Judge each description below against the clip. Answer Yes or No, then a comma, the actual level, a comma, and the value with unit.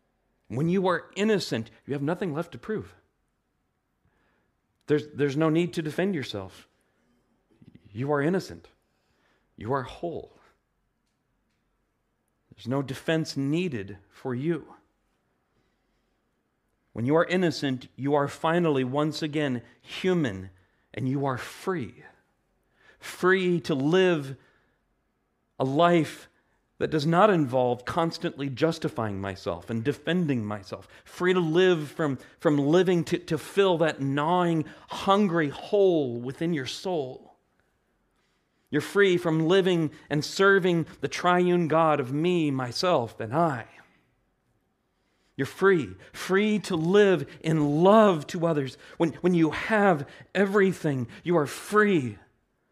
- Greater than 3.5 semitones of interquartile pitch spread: Yes, average, 5.1 semitones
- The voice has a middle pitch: Yes, medium, 155 Hz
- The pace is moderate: No, slow, 120 wpm